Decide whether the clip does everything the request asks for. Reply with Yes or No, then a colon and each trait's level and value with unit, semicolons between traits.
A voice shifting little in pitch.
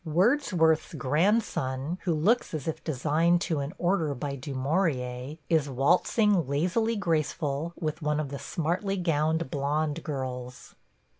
No: average, 3.7 semitones